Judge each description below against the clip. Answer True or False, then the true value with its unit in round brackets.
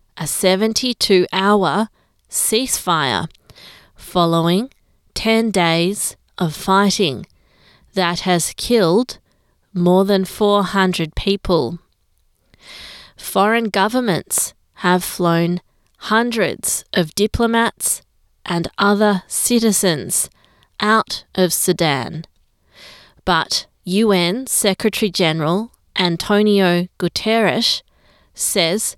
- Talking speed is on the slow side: True (70 wpm)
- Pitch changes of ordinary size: True (3.7 semitones)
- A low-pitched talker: False (195 Hz)